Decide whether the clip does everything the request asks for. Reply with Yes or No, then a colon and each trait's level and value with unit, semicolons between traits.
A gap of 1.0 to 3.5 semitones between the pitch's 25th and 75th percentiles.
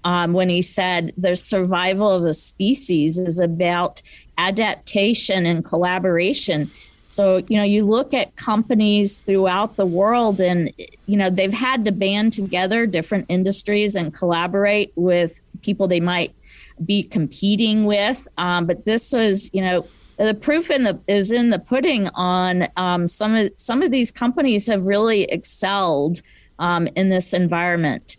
Yes: average, 3.1 semitones